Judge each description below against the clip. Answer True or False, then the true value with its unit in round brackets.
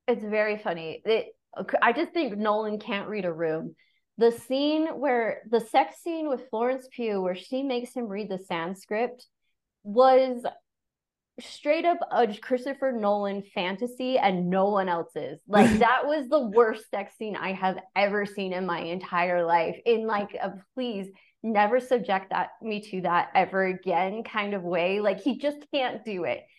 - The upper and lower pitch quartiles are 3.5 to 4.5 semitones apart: False (4.9 semitones)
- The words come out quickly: False (170 wpm)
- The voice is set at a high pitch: True (215 Hz)